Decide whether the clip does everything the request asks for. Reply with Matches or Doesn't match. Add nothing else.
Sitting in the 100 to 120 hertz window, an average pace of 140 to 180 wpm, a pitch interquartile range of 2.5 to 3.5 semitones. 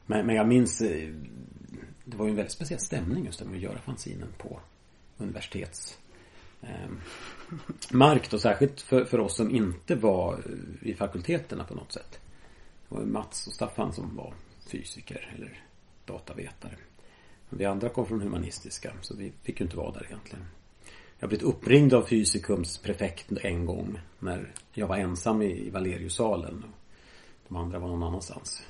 Doesn't match